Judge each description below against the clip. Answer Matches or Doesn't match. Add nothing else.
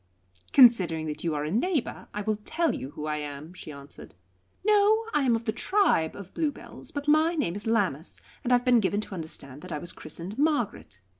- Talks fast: Matches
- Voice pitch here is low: Doesn't match